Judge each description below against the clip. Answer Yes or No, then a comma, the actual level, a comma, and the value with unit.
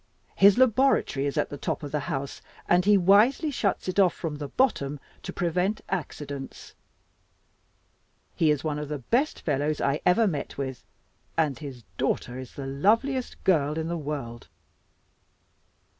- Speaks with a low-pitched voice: No, medium, 155 Hz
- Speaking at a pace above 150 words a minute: Yes, average, 160 wpm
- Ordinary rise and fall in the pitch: No, wide, 6.0 semitones